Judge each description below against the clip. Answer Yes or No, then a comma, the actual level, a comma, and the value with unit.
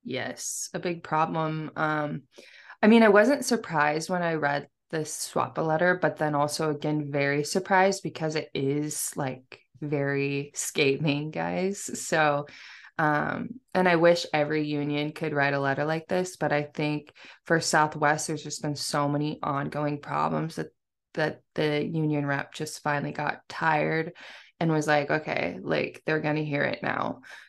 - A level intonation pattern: Yes, narrow, 2.1 semitones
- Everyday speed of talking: Yes, average, 160 wpm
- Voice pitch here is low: No, medium, 150 Hz